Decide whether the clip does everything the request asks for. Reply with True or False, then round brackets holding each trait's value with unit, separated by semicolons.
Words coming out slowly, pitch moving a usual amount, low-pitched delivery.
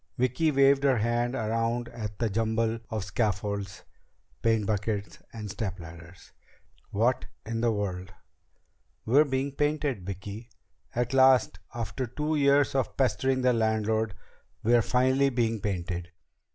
True (130 wpm; 4.0 semitones; 115 Hz)